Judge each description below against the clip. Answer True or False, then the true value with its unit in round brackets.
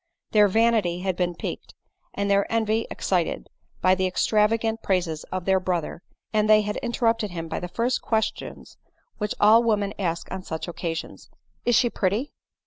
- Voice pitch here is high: True (200 Hz)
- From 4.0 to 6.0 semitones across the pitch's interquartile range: False (3.6 semitones)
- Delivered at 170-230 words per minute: True (175 wpm)